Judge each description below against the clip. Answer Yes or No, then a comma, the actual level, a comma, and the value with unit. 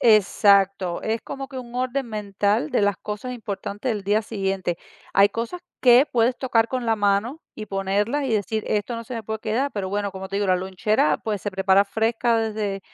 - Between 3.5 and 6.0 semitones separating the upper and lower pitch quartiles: No, average, 2.9 semitones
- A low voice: No, high, 215 Hz